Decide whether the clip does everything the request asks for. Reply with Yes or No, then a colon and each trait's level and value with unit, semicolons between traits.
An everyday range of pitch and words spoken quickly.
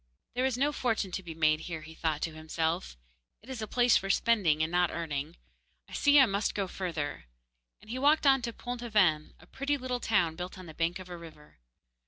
No: wide, 7.1 semitones; fast, 225 wpm